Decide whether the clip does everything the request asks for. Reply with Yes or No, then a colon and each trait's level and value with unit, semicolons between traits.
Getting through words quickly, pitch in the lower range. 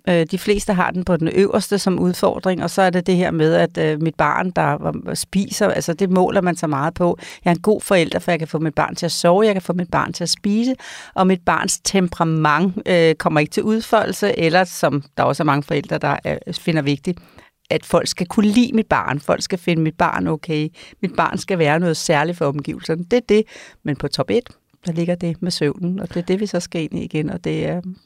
No: fast, 245 wpm; medium, 175 Hz